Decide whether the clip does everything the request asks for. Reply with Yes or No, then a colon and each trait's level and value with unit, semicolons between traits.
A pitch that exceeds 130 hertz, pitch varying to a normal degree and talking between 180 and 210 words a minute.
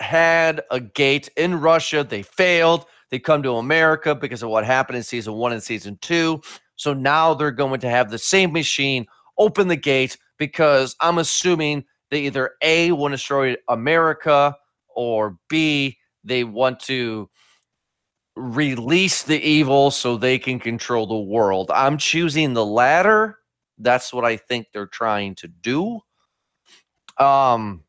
No: medium, 140 Hz; average, 4.7 semitones; average, 150 wpm